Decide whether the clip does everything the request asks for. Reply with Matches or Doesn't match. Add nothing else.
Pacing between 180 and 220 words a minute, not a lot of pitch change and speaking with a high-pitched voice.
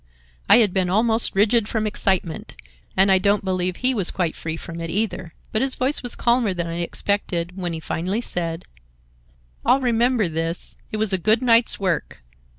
Doesn't match